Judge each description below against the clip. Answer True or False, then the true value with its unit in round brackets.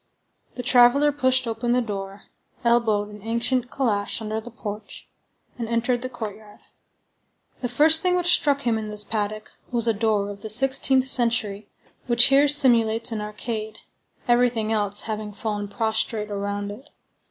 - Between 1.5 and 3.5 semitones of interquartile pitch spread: True (2.8 semitones)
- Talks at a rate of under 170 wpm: True (155 wpm)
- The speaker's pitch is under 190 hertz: False (225 Hz)